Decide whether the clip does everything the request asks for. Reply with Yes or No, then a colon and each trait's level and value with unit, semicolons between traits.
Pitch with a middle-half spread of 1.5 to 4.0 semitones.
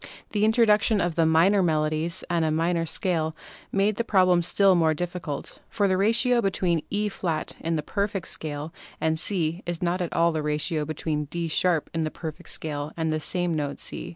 Yes: average, 3.4 semitones